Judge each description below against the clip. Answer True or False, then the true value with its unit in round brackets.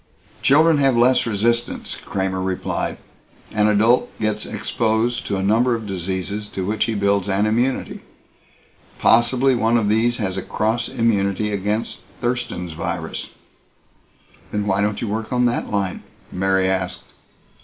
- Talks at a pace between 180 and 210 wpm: False (145 wpm)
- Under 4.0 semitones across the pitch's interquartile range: True (3.4 semitones)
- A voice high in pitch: False (105 Hz)